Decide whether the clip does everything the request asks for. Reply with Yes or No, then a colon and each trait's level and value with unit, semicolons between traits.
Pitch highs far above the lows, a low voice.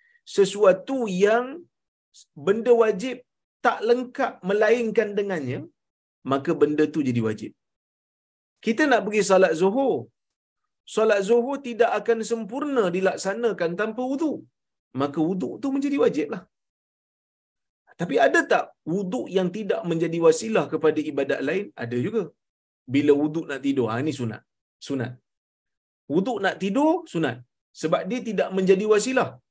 No: wide, 7.3 semitones; high, 195 Hz